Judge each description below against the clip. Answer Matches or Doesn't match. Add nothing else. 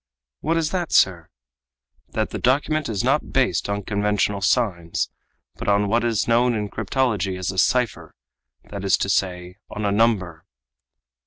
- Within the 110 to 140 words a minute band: Doesn't match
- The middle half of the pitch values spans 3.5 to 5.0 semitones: Matches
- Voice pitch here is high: Doesn't match